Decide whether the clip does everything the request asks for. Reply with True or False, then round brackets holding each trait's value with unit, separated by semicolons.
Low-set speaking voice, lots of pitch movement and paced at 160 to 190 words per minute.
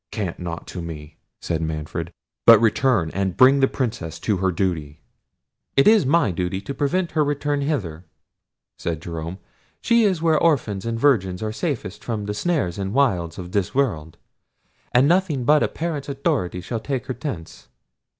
True (110 Hz; 8.2 semitones; 170 wpm)